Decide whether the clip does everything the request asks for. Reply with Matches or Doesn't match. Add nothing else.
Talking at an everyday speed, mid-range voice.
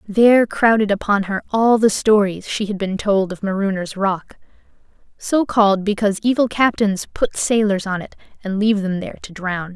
Doesn't match